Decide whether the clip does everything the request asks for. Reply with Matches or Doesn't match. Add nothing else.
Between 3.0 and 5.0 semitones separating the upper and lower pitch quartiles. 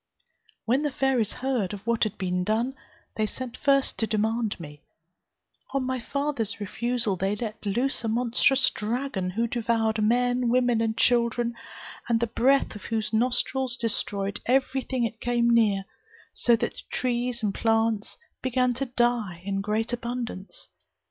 Doesn't match